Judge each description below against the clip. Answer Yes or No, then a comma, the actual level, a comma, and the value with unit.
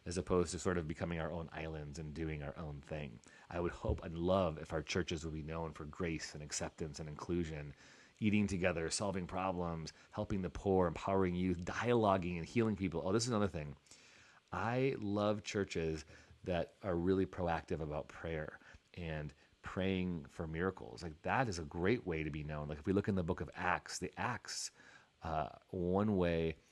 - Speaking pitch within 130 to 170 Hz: No, very low, 85 Hz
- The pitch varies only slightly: No, average, 3.1 semitones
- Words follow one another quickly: No, average, 190 wpm